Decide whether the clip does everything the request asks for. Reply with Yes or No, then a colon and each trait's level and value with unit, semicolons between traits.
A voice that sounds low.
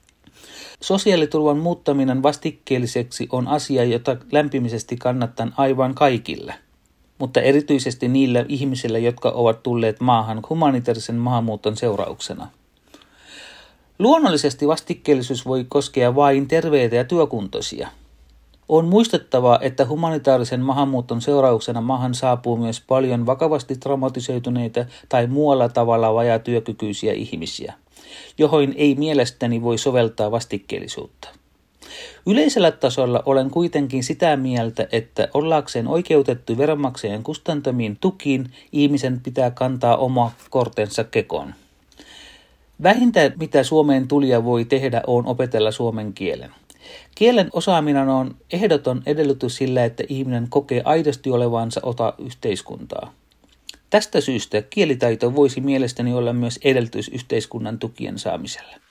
Yes: low, 130 Hz